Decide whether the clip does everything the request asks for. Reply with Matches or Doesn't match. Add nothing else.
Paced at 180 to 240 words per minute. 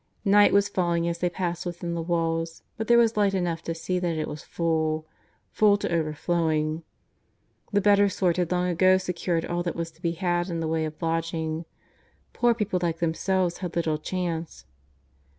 Matches